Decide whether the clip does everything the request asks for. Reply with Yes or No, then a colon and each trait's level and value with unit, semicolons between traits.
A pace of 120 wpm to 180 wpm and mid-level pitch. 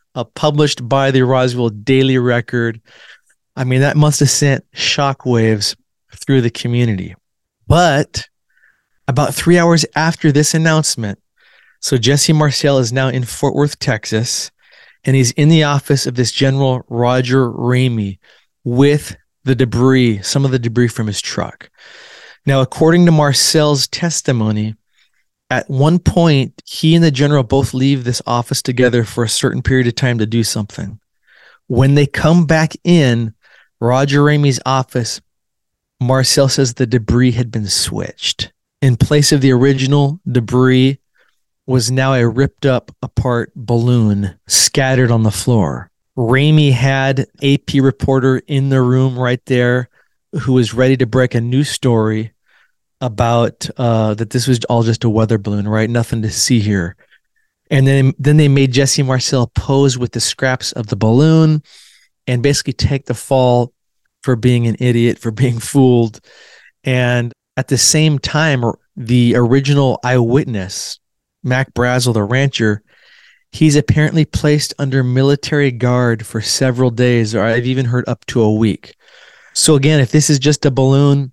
No: average, 155 wpm; low, 130 Hz